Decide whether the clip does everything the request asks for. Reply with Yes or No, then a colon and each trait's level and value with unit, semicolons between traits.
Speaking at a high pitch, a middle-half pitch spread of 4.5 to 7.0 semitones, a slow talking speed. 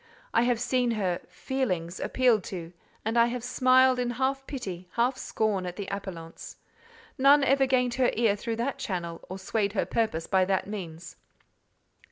No: high, 225 Hz; average, 5.2 semitones; average, 170 wpm